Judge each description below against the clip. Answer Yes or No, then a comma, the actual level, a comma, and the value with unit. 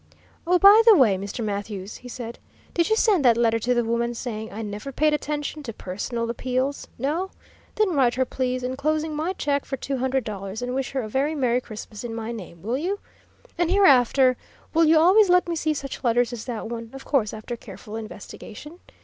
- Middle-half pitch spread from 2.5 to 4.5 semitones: No, average, 4.9 semitones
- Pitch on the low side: No, very high, 255 Hz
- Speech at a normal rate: No, fast, 210 wpm